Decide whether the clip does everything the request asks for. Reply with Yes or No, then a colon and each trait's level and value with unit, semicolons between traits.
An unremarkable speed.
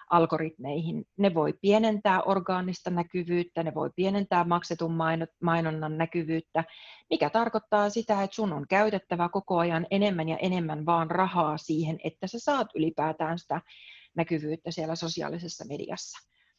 Yes: average, 130 wpm